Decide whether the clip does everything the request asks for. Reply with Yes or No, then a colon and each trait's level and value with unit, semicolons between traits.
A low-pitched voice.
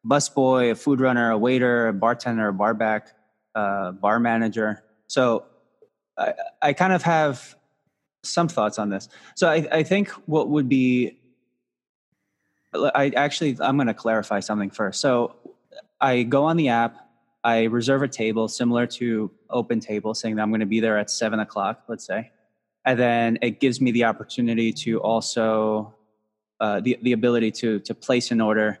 Yes: low, 115 Hz